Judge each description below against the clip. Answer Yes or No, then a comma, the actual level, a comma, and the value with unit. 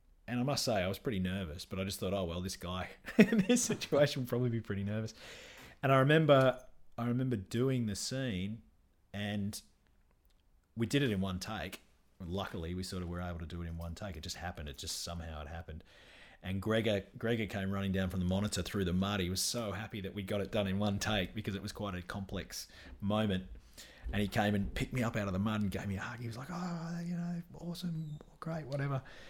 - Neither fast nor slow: No, fast, 235 wpm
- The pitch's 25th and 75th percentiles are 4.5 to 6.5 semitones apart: Yes, average, 5.0 semitones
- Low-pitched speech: Yes, low, 100 Hz